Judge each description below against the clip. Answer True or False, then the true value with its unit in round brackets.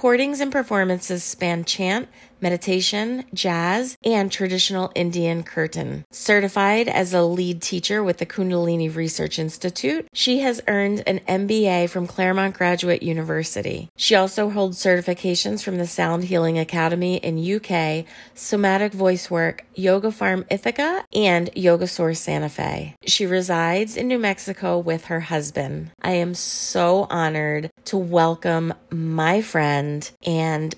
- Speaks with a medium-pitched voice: True (180 Hz)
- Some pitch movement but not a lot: True (3.1 semitones)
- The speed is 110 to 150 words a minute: True (135 wpm)